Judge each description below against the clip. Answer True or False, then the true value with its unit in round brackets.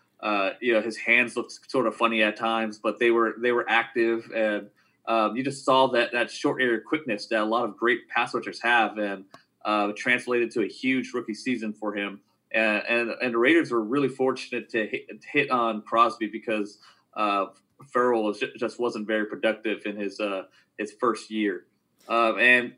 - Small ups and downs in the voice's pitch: True (2.2 semitones)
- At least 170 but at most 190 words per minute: False (200 wpm)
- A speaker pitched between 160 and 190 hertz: False (115 Hz)